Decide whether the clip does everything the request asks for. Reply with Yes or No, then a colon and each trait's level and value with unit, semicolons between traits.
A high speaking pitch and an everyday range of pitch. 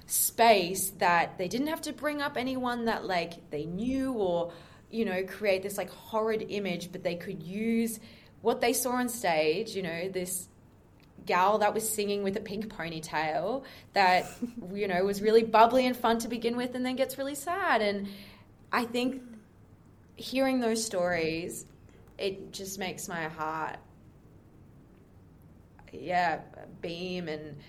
Yes: high, 200 Hz; average, 4.6 semitones